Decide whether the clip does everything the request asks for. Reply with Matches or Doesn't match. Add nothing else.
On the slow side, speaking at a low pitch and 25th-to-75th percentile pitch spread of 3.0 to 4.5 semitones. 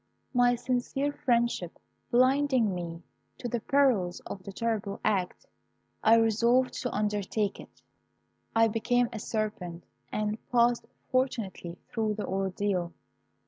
Doesn't match